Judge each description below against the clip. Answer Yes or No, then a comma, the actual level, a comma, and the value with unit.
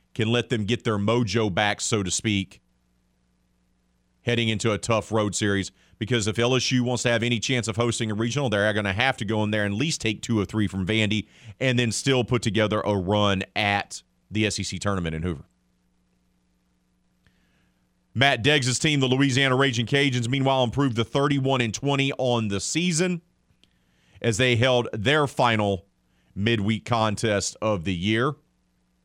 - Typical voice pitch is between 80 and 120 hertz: Yes, low, 110 Hz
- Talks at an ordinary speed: Yes, average, 175 wpm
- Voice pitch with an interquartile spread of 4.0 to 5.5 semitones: Yes, average, 4.6 semitones